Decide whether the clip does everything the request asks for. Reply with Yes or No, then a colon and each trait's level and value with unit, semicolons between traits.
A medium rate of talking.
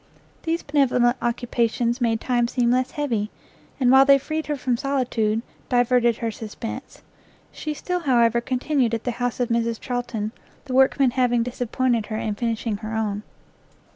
Yes: average, 160 wpm